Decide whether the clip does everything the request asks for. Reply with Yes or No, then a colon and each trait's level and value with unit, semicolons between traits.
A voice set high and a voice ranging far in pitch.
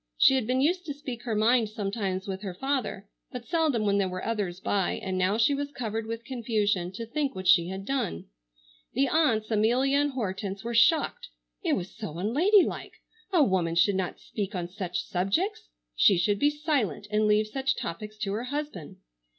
Yes: high, 220 Hz; wide, 5.8 semitones